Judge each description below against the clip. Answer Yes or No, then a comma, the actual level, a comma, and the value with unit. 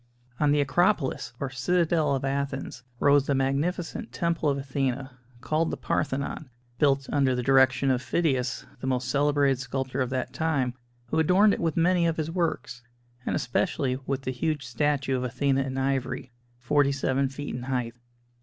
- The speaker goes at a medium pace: Yes, average, 170 wpm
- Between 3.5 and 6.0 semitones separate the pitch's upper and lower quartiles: No, average, 2.7 semitones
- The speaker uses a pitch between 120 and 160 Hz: Yes, medium, 140 Hz